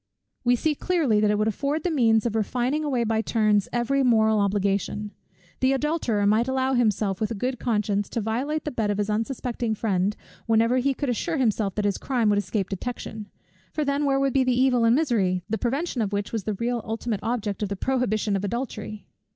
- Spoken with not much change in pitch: No, average, 3.7 semitones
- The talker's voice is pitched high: Yes, high, 230 Hz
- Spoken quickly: Yes, fast, 210 wpm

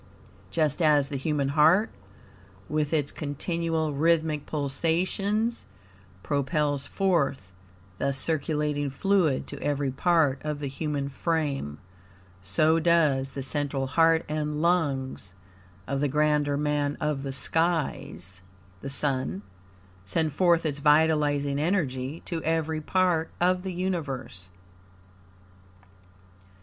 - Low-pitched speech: No, medium, 150 Hz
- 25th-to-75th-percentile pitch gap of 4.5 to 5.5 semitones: No, average, 2.8 semitones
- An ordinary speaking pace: No, slow, 110 wpm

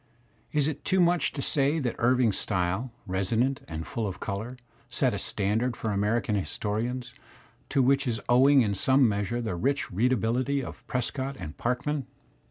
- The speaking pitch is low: Yes, low, 120 Hz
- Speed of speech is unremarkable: Yes, average, 165 wpm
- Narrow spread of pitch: No, average, 4.6 semitones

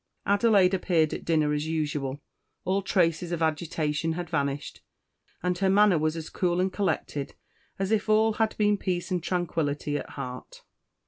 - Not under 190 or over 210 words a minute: No, average, 165 wpm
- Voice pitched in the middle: Yes, medium, 175 Hz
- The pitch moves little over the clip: No, average, 3.9 semitones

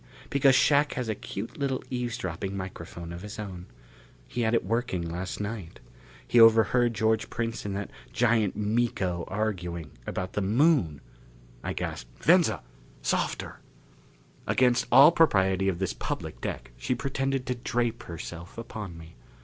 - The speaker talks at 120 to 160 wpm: Yes, average, 150 wpm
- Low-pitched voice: Yes, low, 105 Hz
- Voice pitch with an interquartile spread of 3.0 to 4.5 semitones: No, average, 4.9 semitones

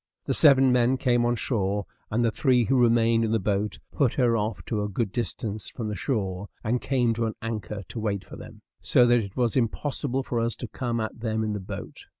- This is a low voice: Yes, low, 115 Hz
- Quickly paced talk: Yes, fast, 230 wpm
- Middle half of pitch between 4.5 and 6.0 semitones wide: No, narrow, 2.5 semitones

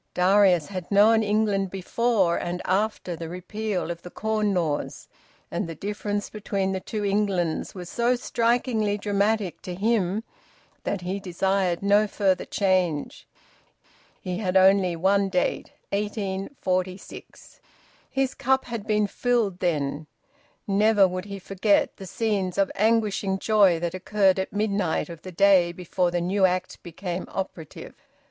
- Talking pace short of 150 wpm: Yes, average, 140 wpm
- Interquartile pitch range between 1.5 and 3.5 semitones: Yes, narrow, 2.5 semitones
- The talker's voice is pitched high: Yes, high, 195 Hz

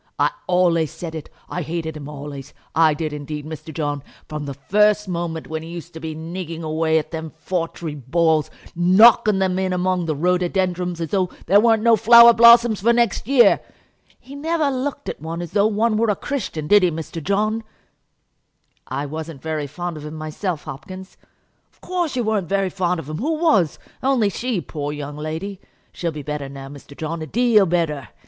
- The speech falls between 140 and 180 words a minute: No, average, 195 wpm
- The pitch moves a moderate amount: Yes, average, 5.0 semitones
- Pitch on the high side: No, medium, 175 Hz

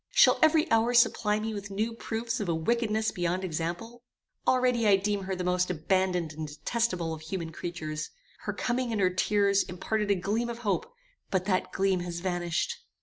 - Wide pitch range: No, average, 4.3 semitones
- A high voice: Yes, high, 195 Hz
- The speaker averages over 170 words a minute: Yes, average, 185 wpm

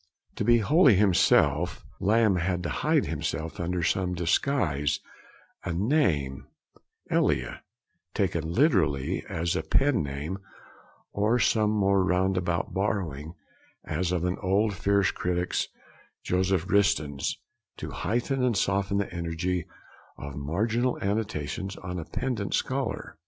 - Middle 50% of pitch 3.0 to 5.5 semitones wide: Yes, average, 3.8 semitones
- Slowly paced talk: Yes, slow, 120 wpm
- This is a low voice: Yes, very low, 95 Hz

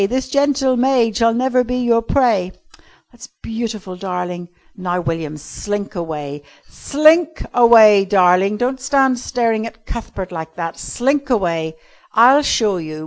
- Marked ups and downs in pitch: Yes, wide, 5.9 semitones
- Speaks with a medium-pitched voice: No, high, 225 Hz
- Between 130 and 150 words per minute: Yes, average, 140 wpm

